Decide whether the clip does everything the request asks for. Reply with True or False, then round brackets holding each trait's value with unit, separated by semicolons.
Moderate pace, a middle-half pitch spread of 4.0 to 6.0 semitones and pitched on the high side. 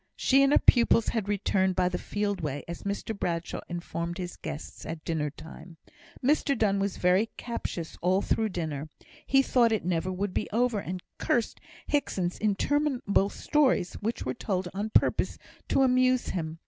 True (170 wpm; 5.0 semitones; 195 Hz)